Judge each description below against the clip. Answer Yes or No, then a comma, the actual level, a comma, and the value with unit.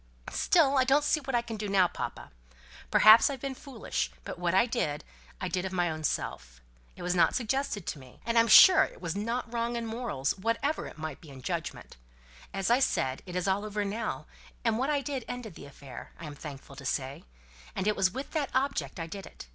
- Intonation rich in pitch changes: Yes, wide, 7.2 semitones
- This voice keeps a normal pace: No, fast, 220 wpm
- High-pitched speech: Yes, high, 205 Hz